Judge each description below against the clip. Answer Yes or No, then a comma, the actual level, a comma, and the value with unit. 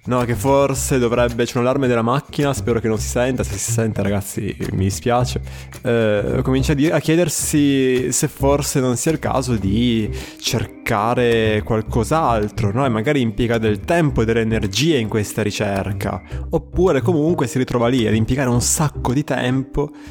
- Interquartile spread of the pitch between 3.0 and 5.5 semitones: Yes, average, 3.9 semitones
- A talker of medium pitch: No, low, 120 Hz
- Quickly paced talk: Yes, fast, 175 wpm